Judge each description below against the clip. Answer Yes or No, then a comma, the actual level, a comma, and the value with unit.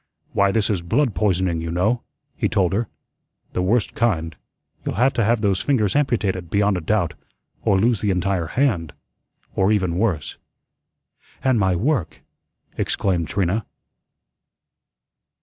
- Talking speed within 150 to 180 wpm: No, average, 140 wpm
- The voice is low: Yes, low, 100 Hz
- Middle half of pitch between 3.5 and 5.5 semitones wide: Yes, average, 4.1 semitones